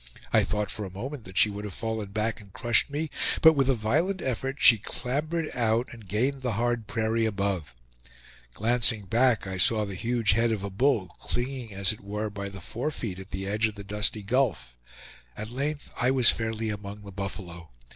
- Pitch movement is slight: No, average, 3.6 semitones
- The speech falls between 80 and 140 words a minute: No, average, 200 wpm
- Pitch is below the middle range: Yes, low, 110 Hz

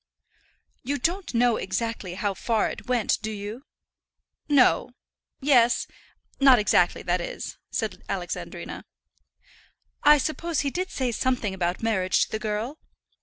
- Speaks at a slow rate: Yes, slow, 130 wpm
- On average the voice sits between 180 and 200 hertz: No, high, 240 Hz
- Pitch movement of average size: Yes, average, 4.7 semitones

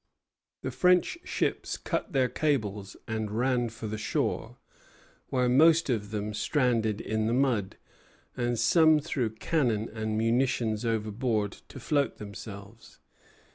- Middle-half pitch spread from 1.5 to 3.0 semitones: No, average, 3.6 semitones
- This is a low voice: Yes, low, 115 Hz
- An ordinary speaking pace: No, slow, 130 wpm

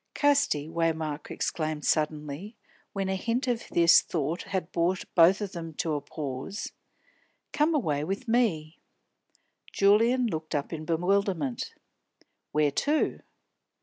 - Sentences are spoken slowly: Yes, slow, 125 wpm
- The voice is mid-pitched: Yes, medium, 170 Hz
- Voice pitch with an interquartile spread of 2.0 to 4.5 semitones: No, average, 5.0 semitones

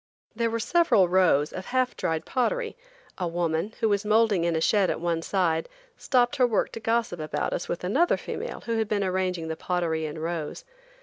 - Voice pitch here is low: No, high, 190 Hz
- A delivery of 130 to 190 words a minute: No, average, 200 wpm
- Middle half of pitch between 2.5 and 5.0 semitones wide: No, wide, 5.5 semitones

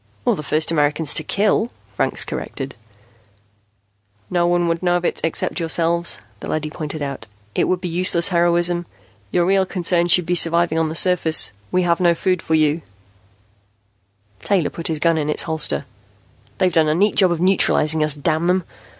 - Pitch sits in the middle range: Yes, medium, 170 Hz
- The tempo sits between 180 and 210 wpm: Yes, average, 185 wpm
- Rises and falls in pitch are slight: Yes, narrow, 2.2 semitones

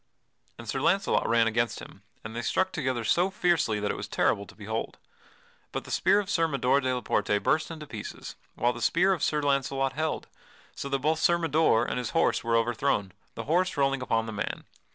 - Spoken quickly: Yes, fast, 215 wpm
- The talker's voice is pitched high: No, low, 135 Hz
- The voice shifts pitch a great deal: Yes, wide, 5.7 semitones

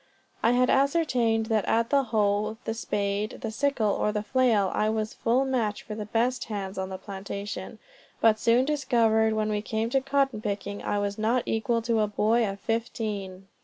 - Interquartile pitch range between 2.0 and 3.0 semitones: Yes, narrow, 2.5 semitones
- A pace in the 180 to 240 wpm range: Yes, average, 195 wpm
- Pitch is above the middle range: Yes, high, 220 Hz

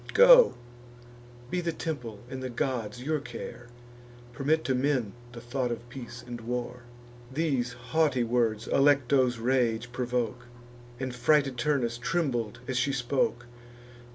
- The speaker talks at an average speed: No, slow, 130 wpm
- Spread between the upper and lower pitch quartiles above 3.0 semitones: No, narrow, 2.5 semitones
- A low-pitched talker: Yes, low, 125 Hz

